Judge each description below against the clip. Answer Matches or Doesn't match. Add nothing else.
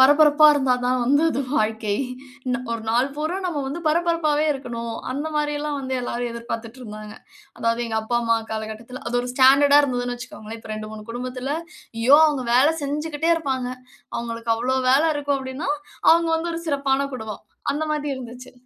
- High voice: Matches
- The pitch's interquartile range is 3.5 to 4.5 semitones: Matches